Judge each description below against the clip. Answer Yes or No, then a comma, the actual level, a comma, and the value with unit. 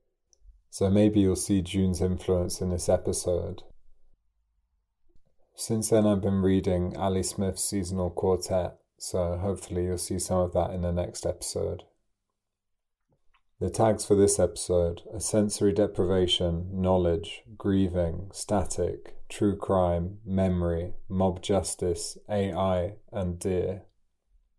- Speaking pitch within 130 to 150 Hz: No, very low, 95 Hz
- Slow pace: Yes, slow, 115 wpm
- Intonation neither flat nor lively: No, narrow, 2.0 semitones